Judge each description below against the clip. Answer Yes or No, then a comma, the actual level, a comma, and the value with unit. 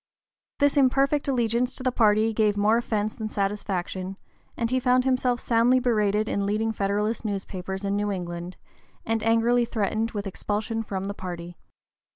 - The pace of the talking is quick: No, average, 160 wpm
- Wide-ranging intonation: No, average, 3.1 semitones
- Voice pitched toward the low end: No, high, 215 Hz